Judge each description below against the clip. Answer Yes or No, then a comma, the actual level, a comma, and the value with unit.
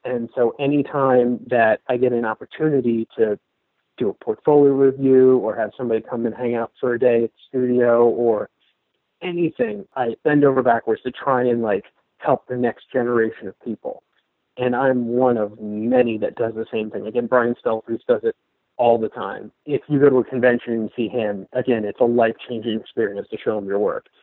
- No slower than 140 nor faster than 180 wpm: No, average, 200 wpm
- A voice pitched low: Yes, low, 125 Hz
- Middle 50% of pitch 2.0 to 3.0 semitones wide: Yes, narrow, 2.6 semitones